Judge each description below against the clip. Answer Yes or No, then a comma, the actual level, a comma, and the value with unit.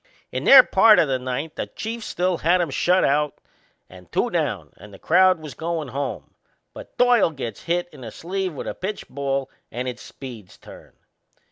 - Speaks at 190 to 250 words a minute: Yes, average, 195 wpm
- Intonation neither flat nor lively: No, wide, 5.9 semitones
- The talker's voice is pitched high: No, medium, 150 Hz